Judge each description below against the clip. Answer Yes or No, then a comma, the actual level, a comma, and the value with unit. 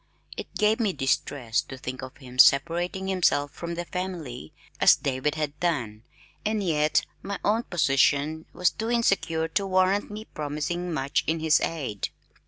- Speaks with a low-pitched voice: No, medium, 160 Hz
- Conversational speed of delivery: Yes, average, 160 wpm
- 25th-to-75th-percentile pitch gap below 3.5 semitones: No, average, 5.0 semitones